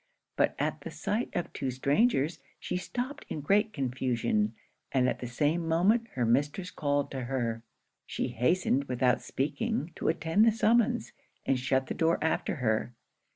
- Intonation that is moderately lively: No, wide, 6.3 semitones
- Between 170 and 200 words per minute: No, average, 160 wpm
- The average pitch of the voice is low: No, medium, 145 Hz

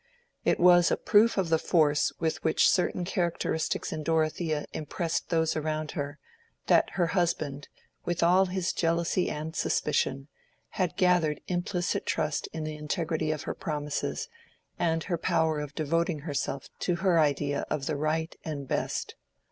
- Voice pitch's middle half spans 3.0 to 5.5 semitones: No, narrow, 2.5 semitones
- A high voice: No, medium, 160 Hz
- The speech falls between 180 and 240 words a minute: No, average, 155 wpm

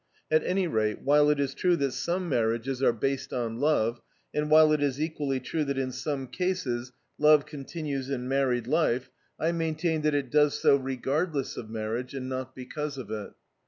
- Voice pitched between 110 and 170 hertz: Yes, medium, 140 Hz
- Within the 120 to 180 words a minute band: No, average, 190 wpm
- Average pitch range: Yes, average, 3.3 semitones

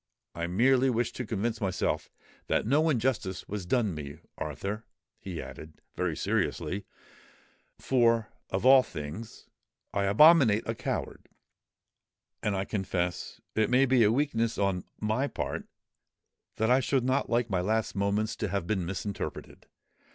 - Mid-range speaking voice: No, low, 110 Hz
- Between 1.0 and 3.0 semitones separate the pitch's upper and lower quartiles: No, average, 4.2 semitones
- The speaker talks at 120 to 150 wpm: Yes, slow, 135 wpm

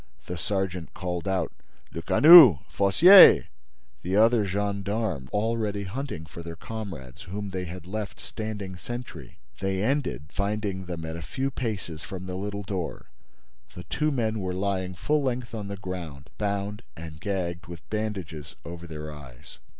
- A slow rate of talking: No, average, 155 wpm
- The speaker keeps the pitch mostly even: No, average, 3.7 semitones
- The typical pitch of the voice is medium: No, very low, 95 Hz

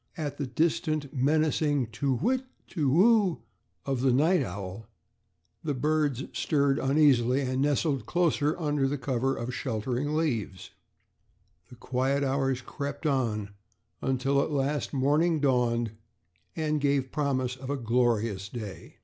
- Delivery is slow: Yes, slow, 130 wpm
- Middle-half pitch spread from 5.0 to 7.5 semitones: No, average, 3.1 semitones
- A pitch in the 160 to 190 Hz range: No, low, 135 Hz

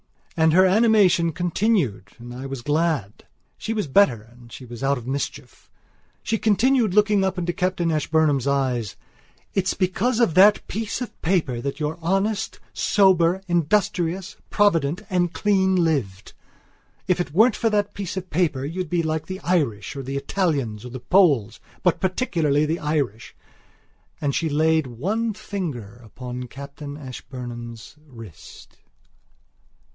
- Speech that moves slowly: No, average, 145 wpm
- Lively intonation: Yes, wide, 6.2 semitones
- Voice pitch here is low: No, medium, 160 Hz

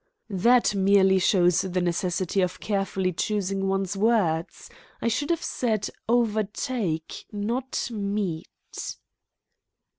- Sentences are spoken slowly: Yes, slow, 100 wpm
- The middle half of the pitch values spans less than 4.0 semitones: Yes, average, 3.1 semitones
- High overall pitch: Yes, high, 195 Hz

